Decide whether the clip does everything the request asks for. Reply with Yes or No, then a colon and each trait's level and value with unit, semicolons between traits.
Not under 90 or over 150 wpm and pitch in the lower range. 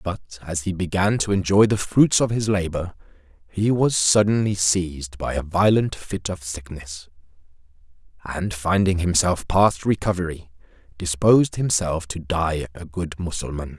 Yes: average, 145 wpm; very low, 90 Hz